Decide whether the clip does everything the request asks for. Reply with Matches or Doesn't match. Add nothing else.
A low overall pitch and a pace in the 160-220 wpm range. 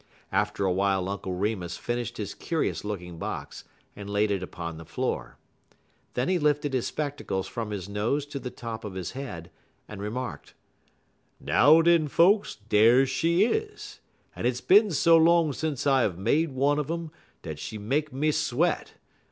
Matches